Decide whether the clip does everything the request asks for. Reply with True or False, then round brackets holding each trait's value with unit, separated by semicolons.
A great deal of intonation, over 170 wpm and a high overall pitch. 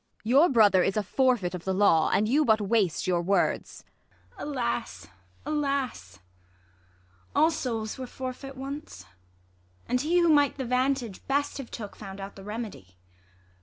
False (5.7 semitones; 160 wpm; 235 Hz)